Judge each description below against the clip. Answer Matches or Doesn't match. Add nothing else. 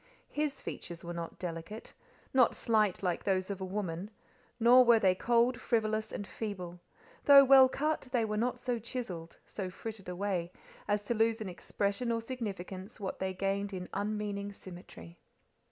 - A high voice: Matches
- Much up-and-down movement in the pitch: Doesn't match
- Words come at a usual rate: Matches